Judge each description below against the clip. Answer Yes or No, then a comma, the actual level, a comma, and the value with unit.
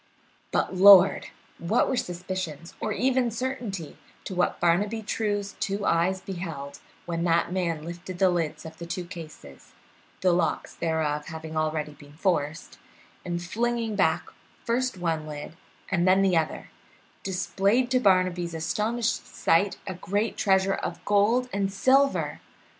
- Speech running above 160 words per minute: No, average, 140 wpm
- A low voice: No, medium, 185 Hz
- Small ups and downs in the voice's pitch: No, average, 3.5 semitones